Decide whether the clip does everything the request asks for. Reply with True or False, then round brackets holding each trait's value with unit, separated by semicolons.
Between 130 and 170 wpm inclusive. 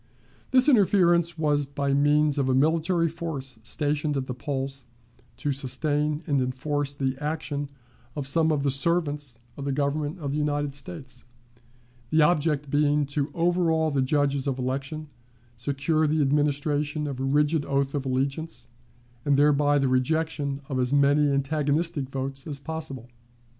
True (155 wpm)